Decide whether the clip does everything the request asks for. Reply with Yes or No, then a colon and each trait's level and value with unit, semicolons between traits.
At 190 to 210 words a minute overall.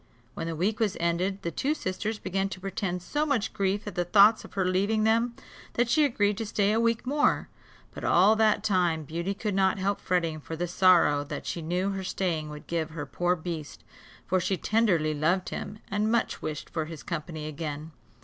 Yes: fast, 205 wpm